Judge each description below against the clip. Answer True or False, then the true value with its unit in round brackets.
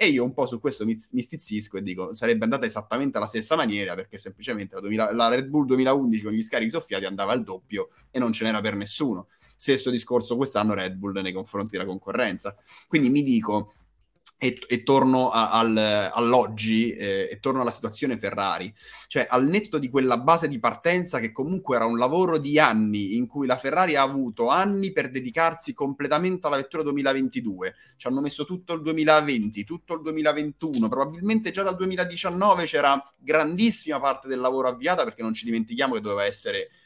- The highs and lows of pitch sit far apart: True (6.3 semitones)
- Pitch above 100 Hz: True (135 Hz)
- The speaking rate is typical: False (185 wpm)